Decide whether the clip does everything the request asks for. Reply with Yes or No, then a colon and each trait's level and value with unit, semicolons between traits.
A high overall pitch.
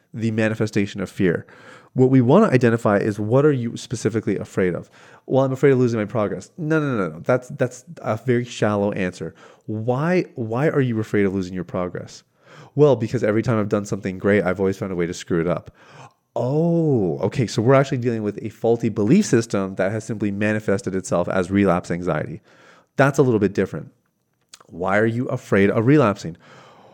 No: low, 115 Hz